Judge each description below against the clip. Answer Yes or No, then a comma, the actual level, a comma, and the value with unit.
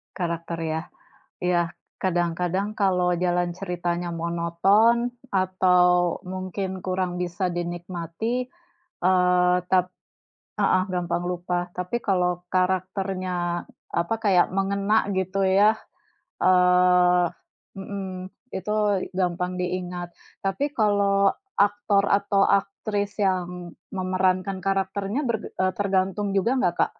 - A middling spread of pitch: No, narrow, 1.8 semitones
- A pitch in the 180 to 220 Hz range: Yes, medium, 185 Hz